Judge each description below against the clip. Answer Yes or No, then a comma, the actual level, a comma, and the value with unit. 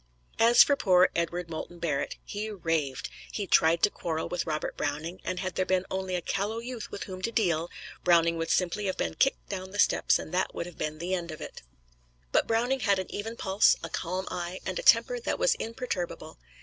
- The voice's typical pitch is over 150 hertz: Yes, medium, 185 Hz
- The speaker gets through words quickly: Yes, fast, 215 wpm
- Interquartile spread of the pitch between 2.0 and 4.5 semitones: Yes, average, 3.5 semitones